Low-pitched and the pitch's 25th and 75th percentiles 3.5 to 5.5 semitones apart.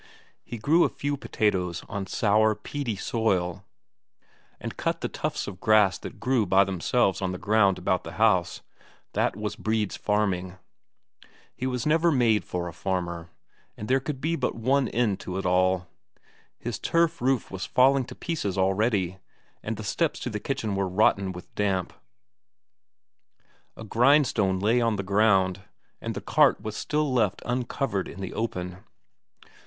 Yes: low, 105 Hz; average, 4.5 semitones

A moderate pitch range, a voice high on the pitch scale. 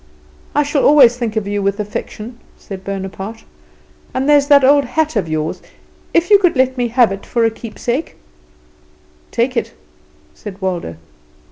No: wide, 5.7 semitones; high, 235 Hz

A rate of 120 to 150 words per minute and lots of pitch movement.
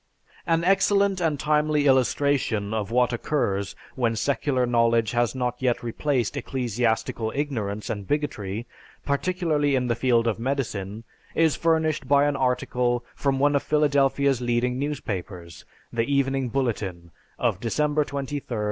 No: average, 140 wpm; average, 3.9 semitones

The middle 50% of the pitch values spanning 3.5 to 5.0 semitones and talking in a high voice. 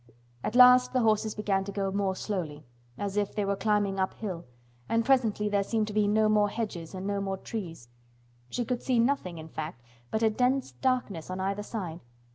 No: average, 2.9 semitones; high, 205 Hz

